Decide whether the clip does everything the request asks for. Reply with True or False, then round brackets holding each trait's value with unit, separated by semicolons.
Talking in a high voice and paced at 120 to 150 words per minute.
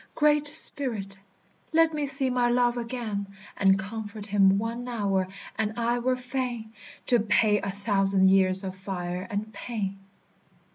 True (220 Hz; 145 wpm)